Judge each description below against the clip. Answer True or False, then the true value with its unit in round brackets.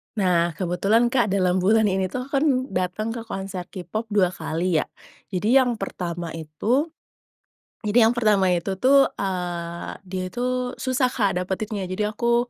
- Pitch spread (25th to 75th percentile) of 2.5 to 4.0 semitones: False (4.6 semitones)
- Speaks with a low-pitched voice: False (195 Hz)